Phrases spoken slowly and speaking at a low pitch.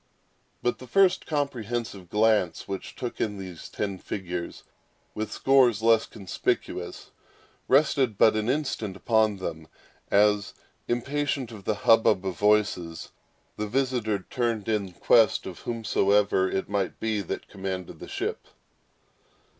Yes: slow, 130 wpm; low, 105 Hz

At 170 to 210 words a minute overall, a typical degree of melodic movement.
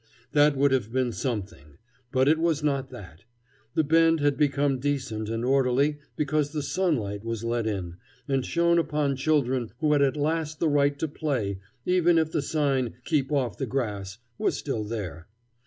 Yes: average, 175 wpm; average, 4.5 semitones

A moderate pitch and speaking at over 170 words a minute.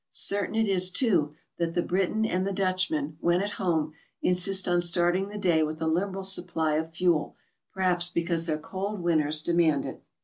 Yes: medium, 175 Hz; average, 180 wpm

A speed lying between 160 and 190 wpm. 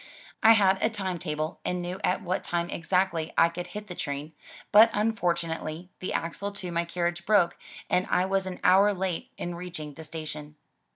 Yes: average, 185 wpm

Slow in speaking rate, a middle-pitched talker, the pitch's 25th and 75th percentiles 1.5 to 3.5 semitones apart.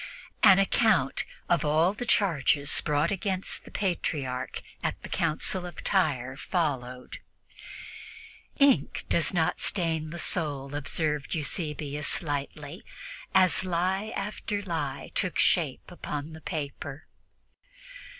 No: slow, 110 wpm; medium, 160 Hz; average, 4.3 semitones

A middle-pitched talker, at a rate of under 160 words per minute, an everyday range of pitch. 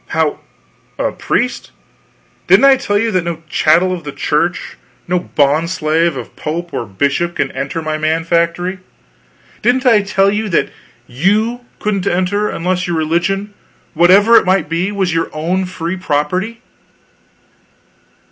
Yes: medium, 175 Hz; average, 145 wpm; average, 3.5 semitones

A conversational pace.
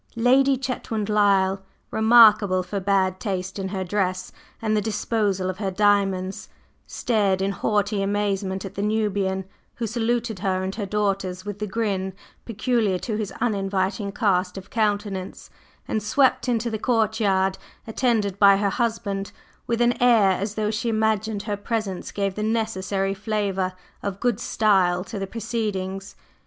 Yes: average, 150 wpm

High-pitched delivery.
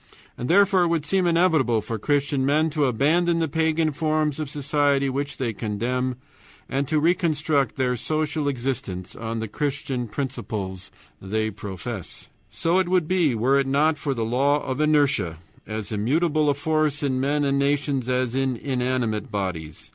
No: medium, 140 Hz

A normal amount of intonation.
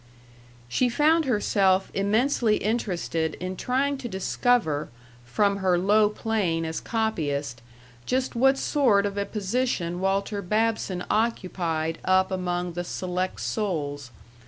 Yes: average, 4.4 semitones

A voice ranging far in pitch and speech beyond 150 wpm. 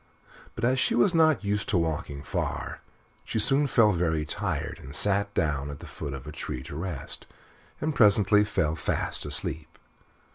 Yes: wide, 6.1 semitones; average, 175 wpm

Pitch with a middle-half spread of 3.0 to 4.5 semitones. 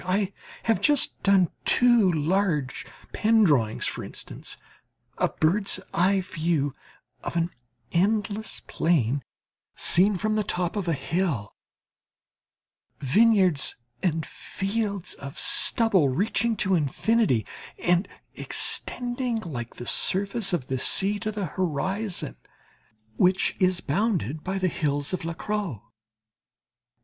No: average, 4.9 semitones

